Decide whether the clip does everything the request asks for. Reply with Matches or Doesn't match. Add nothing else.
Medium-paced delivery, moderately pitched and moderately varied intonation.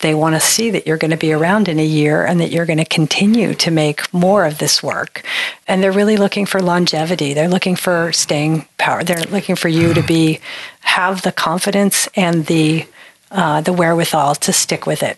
Doesn't match